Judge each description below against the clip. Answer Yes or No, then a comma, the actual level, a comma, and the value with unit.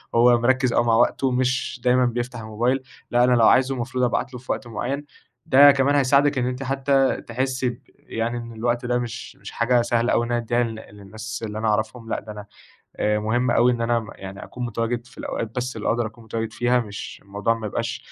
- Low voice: Yes, low, 120 Hz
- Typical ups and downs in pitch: No, narrow, 2.0 semitones